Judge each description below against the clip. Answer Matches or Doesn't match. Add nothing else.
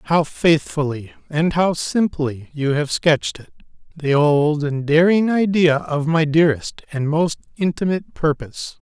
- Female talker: Doesn't match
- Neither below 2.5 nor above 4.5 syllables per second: Matches